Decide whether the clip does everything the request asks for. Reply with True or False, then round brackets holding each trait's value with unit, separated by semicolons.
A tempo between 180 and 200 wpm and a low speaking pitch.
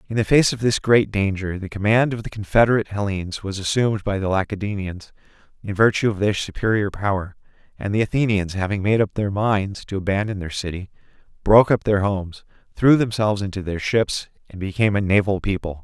True (190 wpm; 100 Hz)